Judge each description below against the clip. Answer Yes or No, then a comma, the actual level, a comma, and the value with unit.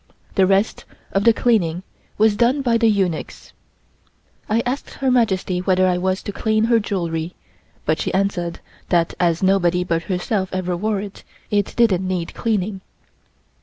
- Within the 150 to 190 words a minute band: Yes, average, 160 wpm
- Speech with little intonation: No, average, 3.4 semitones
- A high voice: Yes, high, 195 Hz